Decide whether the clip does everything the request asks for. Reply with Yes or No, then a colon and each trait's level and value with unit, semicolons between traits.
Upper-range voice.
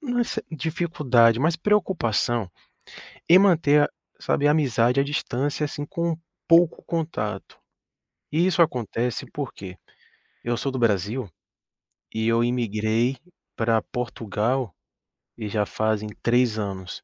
No: low, 125 Hz